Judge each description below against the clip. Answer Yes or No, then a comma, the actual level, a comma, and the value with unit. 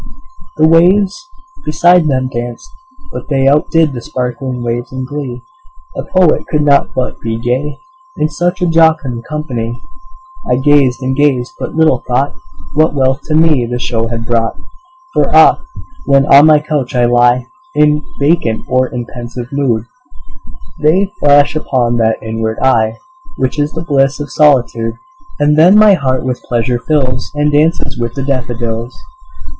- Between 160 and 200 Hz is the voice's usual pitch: No, low, 135 Hz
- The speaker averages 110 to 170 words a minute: Yes, average, 160 wpm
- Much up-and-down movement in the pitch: No, average, 3.8 semitones